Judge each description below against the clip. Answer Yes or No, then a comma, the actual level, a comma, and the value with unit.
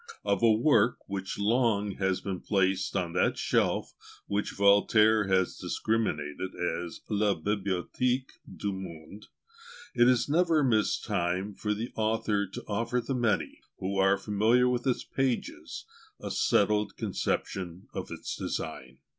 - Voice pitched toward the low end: Yes, low, 105 Hz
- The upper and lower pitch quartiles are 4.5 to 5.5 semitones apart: No, average, 3.4 semitones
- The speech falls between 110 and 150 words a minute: Yes, slow, 135 wpm